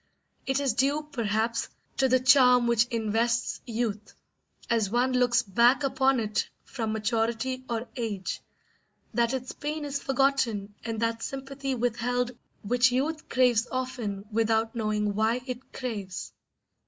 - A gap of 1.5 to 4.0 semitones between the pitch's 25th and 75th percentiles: Yes, narrow, 2.6 semitones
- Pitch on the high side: Yes, high, 240 Hz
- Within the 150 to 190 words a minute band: No, slow, 135 wpm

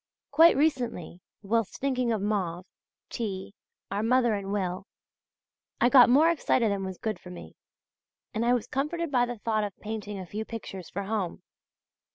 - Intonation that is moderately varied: Yes, average, 4.1 semitones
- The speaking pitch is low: No, high, 220 Hz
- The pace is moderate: Yes, average, 170 wpm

